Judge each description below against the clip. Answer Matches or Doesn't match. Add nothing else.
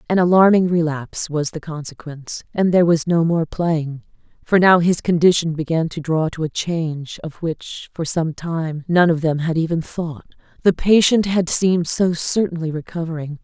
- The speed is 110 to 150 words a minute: Doesn't match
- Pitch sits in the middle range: Matches